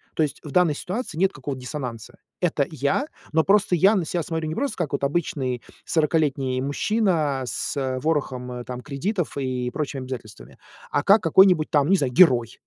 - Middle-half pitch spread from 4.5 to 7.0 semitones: Yes, average, 5.1 semitones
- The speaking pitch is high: No, medium, 150 Hz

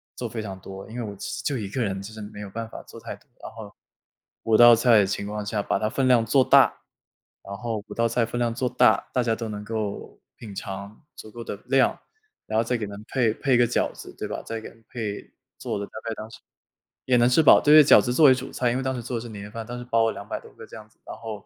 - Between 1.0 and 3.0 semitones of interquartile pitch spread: Yes, average, 2.7 semitones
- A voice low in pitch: Yes, low, 115 Hz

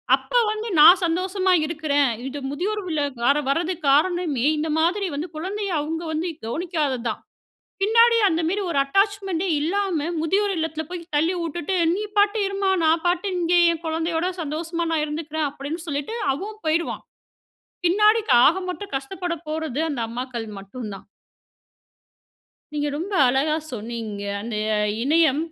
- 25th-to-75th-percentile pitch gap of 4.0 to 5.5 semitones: Yes, average, 4.3 semitones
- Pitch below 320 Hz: No, very high, 325 Hz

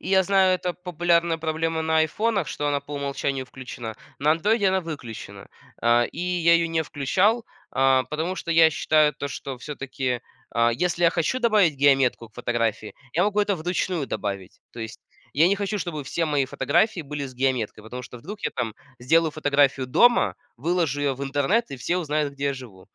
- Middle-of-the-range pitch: Yes, medium, 150 Hz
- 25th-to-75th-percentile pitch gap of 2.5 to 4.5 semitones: No, average, 4.9 semitones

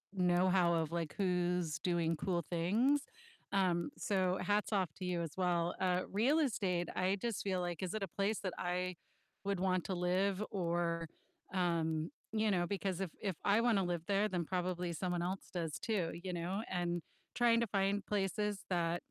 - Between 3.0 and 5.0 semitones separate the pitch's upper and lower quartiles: No, narrow, 2.4 semitones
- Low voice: No, medium, 180 Hz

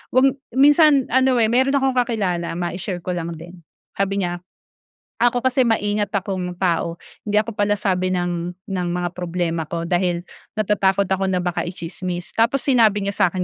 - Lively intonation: No, average, 4.2 semitones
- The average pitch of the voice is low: No, high, 190 Hz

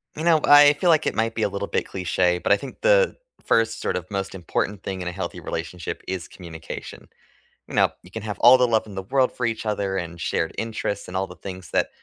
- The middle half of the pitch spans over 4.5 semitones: No, average, 4.1 semitones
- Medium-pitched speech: No, low, 100 Hz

